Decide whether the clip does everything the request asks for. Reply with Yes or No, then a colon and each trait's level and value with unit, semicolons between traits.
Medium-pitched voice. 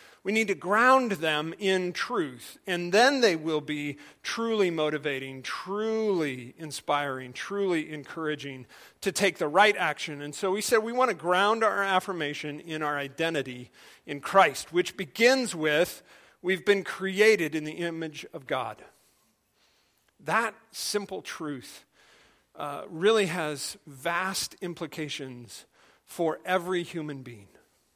Yes: medium, 170 Hz